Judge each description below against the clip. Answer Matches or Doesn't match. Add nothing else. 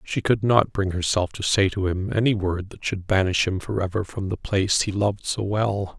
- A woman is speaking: Doesn't match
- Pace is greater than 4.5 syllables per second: Matches